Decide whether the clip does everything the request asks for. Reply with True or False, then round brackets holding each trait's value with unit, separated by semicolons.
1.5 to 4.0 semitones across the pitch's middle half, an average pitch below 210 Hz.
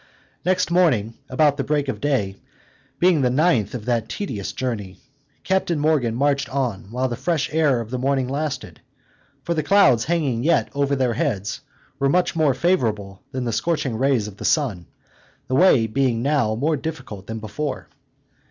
False (5.0 semitones; 135 Hz)